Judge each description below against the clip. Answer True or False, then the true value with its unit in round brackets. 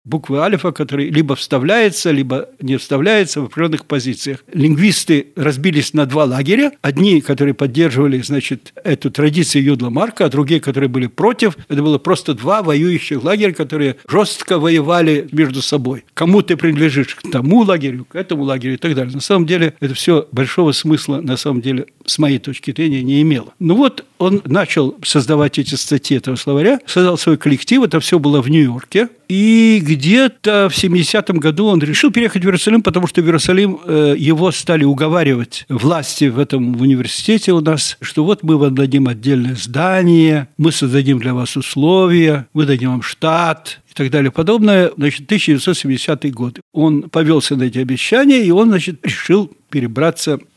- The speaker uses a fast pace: True (165 wpm)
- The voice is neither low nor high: True (155 Hz)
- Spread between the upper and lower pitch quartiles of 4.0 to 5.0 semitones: True (4.3 semitones)